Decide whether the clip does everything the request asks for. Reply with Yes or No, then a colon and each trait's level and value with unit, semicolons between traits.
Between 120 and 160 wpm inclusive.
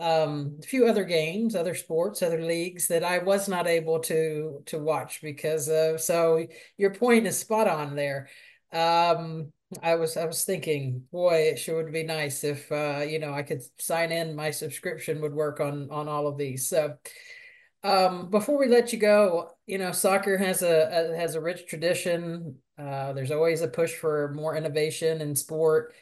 No: average, 190 wpm